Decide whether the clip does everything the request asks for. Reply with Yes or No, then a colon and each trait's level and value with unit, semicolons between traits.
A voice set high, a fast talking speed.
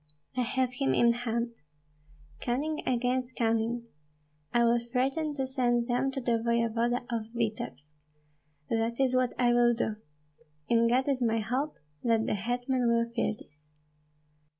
No: high, 240 Hz; average, 150 wpm